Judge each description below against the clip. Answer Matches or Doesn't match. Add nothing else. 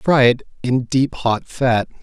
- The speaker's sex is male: Matches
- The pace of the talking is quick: Doesn't match